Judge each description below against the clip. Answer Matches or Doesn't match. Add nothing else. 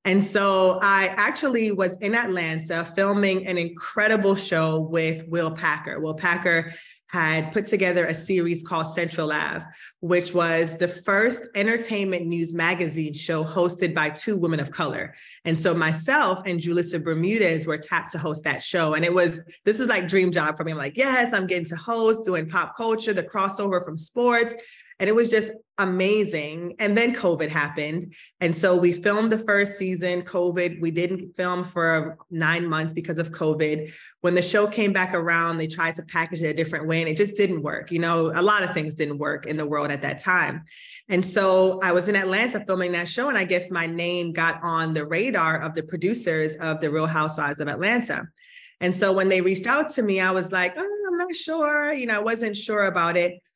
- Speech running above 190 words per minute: Matches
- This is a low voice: Doesn't match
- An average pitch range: Matches